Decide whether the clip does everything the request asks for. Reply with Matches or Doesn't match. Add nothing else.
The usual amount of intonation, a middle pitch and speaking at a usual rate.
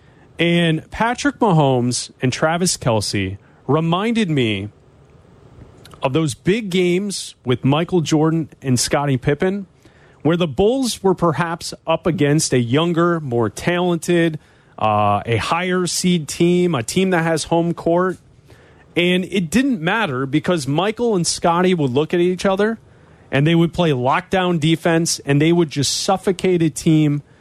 Matches